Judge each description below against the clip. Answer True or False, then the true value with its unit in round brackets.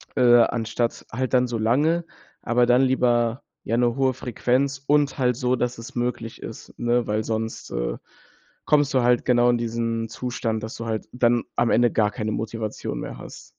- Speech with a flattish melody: True (1.7 semitones)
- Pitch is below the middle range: True (120 Hz)